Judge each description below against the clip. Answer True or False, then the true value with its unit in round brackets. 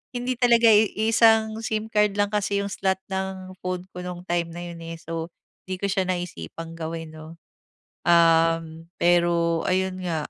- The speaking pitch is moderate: True (180 Hz)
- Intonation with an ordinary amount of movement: True (3.5 semitones)